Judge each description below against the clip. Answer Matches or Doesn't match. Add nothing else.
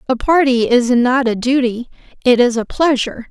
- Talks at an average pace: Matches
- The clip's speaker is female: Matches